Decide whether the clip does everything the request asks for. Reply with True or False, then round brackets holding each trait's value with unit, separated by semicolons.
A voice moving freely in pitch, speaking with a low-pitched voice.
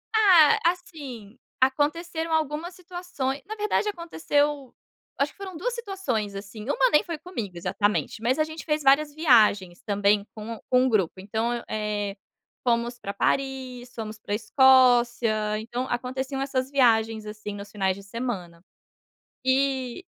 False (5.9 semitones; 255 Hz)